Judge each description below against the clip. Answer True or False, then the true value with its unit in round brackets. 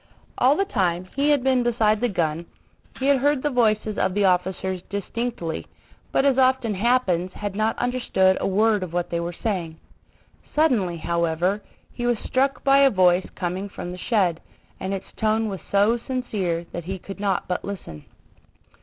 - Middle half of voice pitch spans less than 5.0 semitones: False (5.3 semitones)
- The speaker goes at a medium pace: True (180 wpm)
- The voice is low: False (200 Hz)